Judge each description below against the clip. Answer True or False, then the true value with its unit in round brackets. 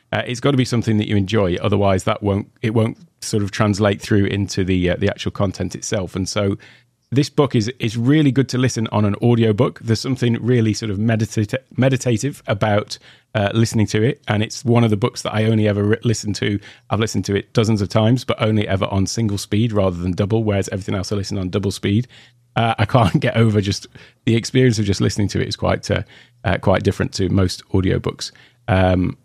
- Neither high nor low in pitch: False (110 Hz)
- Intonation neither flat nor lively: True (3.0 semitones)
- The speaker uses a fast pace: True (230 wpm)